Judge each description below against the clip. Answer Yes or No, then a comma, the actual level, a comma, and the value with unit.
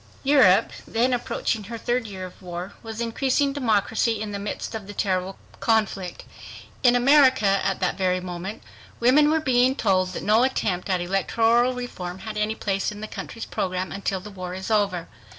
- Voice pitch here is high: Yes, high, 210 Hz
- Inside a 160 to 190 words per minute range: Yes, average, 180 wpm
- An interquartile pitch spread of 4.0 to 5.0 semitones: Yes, average, 4.3 semitones